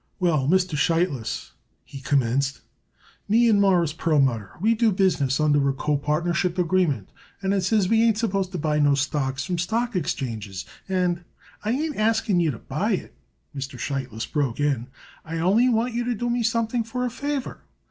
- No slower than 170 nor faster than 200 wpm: Yes, average, 180 wpm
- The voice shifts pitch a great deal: Yes, wide, 7.7 semitones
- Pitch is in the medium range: Yes, medium, 175 Hz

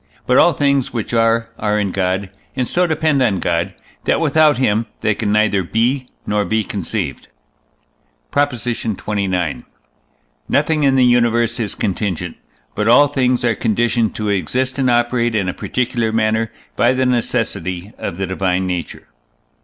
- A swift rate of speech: No, average, 155 wpm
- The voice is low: Yes, low, 115 Hz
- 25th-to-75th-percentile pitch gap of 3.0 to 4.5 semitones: Yes, average, 4.0 semitones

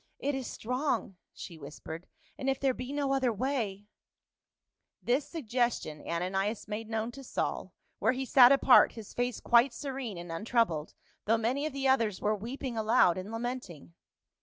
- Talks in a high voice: Yes, high, 235 Hz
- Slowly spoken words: No, average, 175 wpm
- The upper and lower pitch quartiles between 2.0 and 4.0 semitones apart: No, average, 4.4 semitones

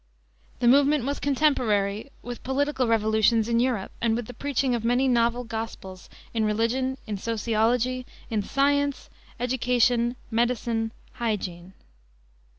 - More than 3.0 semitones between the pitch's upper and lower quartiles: No, narrow, 2.5 semitones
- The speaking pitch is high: Yes, high, 235 Hz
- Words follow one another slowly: Yes, slow, 130 wpm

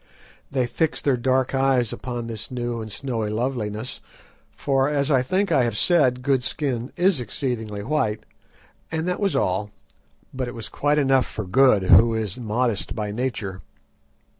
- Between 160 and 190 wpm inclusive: Yes, average, 165 wpm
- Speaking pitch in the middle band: No, low, 125 Hz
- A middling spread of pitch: Yes, average, 3.8 semitones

